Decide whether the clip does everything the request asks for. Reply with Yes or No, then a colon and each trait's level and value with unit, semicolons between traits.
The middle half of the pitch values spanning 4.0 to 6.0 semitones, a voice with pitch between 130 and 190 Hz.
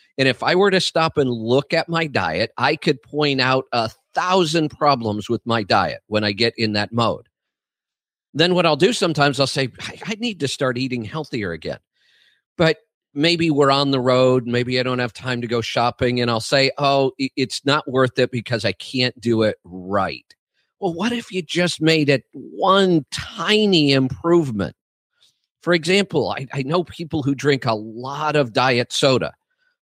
Yes: average, 5.0 semitones; medium, 140 Hz